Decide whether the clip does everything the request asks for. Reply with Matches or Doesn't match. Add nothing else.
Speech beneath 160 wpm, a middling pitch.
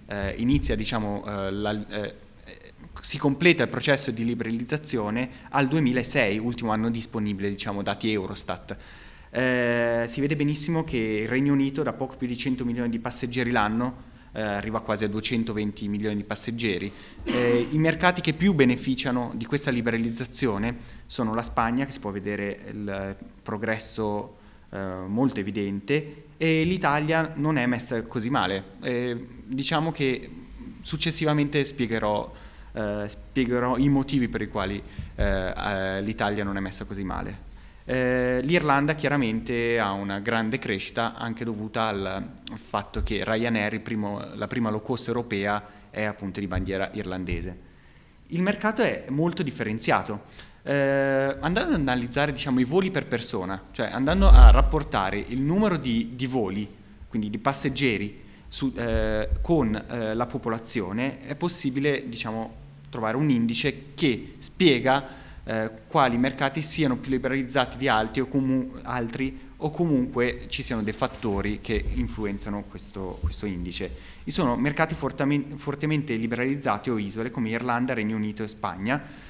Doesn't match